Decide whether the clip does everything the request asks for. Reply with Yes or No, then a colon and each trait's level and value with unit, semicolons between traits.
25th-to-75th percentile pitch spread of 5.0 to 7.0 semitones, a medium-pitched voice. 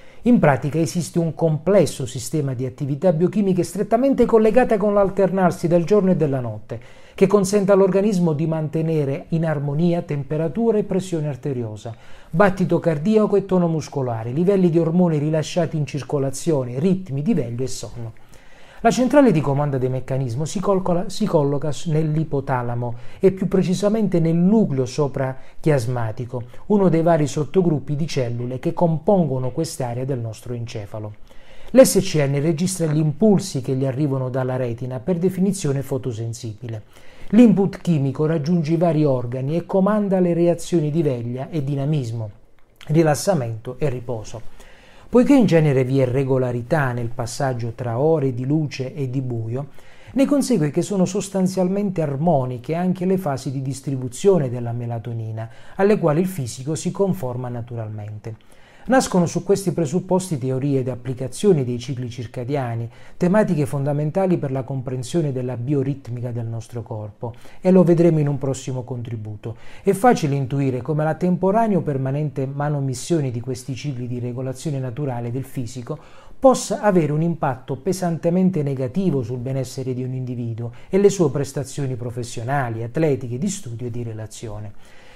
Yes: wide, 5.6 semitones; medium, 145 Hz